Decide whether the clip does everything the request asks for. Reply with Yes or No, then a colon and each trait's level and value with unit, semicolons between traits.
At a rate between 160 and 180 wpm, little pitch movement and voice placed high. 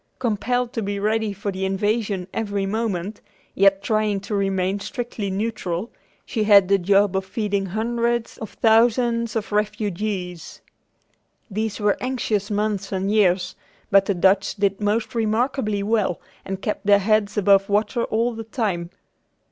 No: average, 145 wpm; narrow, 2.2 semitones; high, 205 Hz